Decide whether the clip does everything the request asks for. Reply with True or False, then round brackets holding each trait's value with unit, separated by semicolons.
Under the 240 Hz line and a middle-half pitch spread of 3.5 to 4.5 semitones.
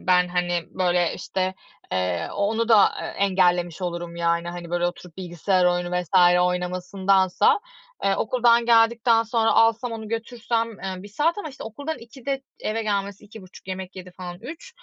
True (190 Hz; 4.2 semitones)